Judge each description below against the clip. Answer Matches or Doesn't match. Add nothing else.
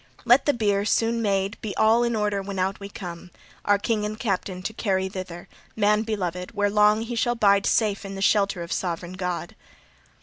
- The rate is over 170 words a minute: Matches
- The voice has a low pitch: Doesn't match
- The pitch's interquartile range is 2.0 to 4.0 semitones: Matches